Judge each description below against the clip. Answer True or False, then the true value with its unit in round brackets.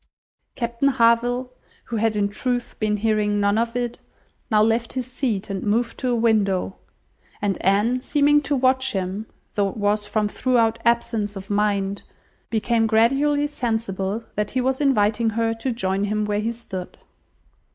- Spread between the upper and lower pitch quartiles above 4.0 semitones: False (2.9 semitones)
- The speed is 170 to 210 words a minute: False (160 wpm)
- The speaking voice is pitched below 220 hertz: False (225 Hz)